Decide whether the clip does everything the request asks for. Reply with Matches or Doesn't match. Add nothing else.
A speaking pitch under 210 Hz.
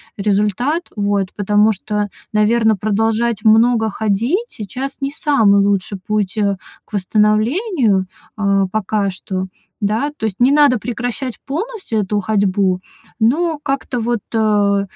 Doesn't match